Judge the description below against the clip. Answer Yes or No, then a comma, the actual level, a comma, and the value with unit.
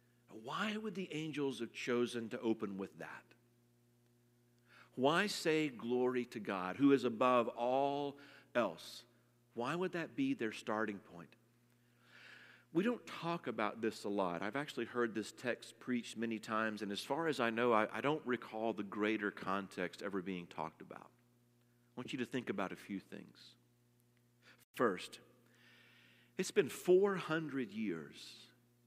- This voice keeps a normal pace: Yes, average, 150 wpm